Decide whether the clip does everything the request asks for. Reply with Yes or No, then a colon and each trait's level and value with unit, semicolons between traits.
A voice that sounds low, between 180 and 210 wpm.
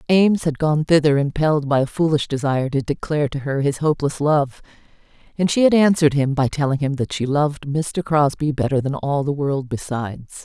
No: medium, 145 Hz; average, 200 wpm